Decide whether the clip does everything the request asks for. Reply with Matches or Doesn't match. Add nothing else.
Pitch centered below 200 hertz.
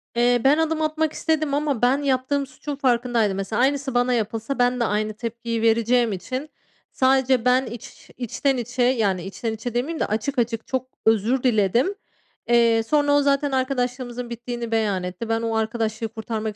Doesn't match